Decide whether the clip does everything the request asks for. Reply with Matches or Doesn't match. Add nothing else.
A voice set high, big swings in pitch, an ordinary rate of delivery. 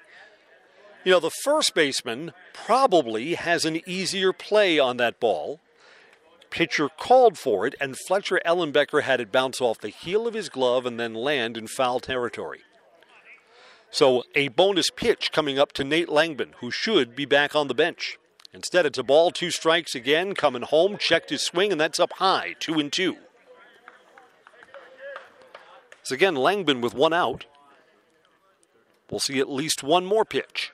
Doesn't match